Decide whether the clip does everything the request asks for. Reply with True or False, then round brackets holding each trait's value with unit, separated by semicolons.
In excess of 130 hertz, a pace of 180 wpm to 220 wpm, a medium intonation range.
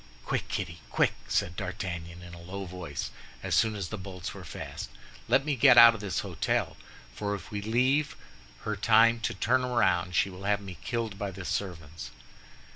False (100 Hz; 190 wpm; 4.2 semitones)